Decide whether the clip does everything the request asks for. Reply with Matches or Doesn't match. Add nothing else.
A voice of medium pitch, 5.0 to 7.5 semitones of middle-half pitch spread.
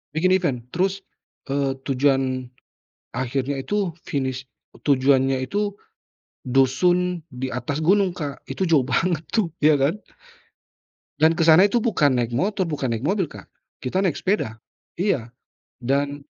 Matches